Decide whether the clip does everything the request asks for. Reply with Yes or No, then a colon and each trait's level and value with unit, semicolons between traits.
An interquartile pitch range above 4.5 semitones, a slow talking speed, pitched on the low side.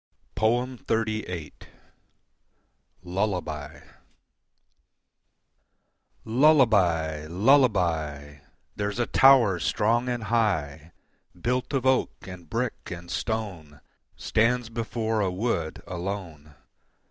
Yes: wide, 5.6 semitones; slow, 75 wpm; low, 105 Hz